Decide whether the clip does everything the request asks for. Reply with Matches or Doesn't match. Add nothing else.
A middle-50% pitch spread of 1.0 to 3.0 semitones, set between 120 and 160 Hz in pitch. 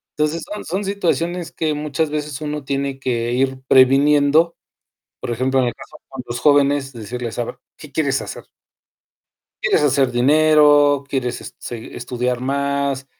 Matches